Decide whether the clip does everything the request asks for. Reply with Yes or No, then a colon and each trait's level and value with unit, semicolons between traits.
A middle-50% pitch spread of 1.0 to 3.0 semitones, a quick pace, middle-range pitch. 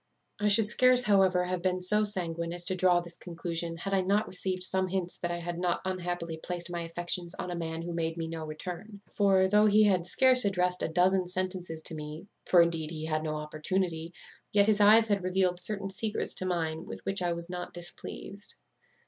Yes: narrow, 2.4 semitones; fast, 210 wpm; medium, 180 Hz